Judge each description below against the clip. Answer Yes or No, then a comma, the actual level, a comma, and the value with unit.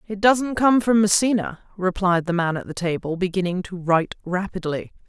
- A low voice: No, high, 190 Hz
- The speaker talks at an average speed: Yes, average, 175 wpm